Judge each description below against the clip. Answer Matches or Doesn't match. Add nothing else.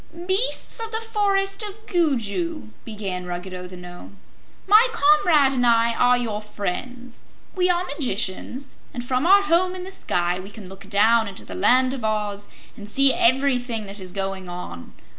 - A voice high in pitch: Matches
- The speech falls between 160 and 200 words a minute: Matches